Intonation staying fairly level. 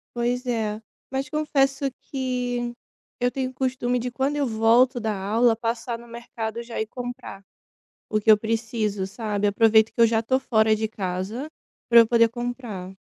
Yes: narrow, 2.2 semitones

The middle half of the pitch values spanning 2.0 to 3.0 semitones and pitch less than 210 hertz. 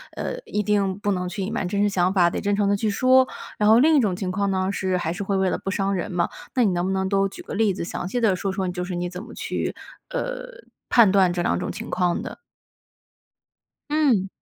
Yes: narrow, 2.4 semitones; high, 195 Hz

